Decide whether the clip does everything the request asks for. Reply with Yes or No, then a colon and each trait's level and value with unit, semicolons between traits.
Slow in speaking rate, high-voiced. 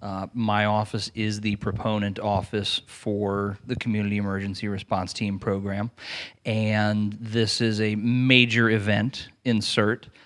No: slow, 125 wpm; low, 105 Hz